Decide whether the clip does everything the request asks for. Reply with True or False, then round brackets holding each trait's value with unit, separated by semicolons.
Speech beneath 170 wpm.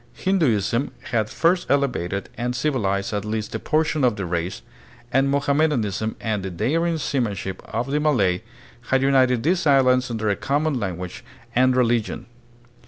True (160 wpm)